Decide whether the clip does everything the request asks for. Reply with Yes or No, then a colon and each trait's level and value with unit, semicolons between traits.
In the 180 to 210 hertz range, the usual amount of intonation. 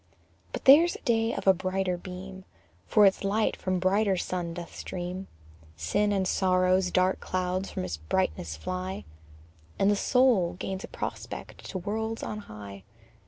No: medium, 185 Hz; narrow, 2.2 semitones